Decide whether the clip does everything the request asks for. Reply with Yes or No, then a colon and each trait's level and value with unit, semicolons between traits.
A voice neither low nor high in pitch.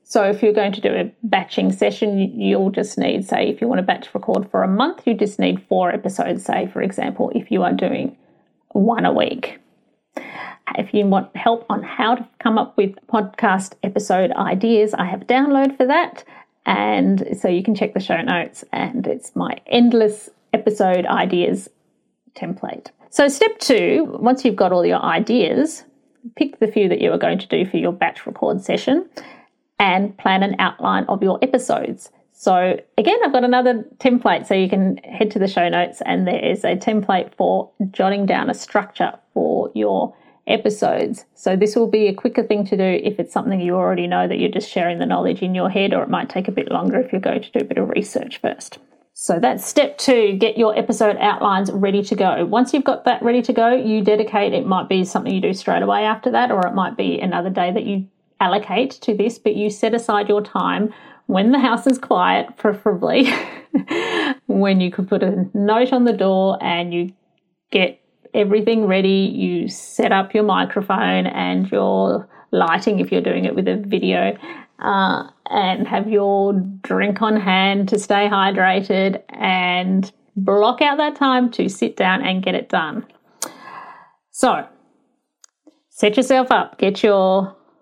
No: high, 210 Hz